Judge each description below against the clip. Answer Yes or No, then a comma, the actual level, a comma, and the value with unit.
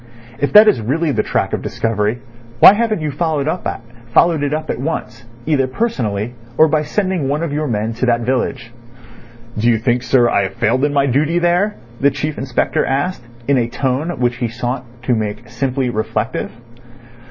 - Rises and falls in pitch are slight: No, average, 4.6 semitones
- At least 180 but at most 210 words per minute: Yes, average, 185 wpm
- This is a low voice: Yes, low, 130 Hz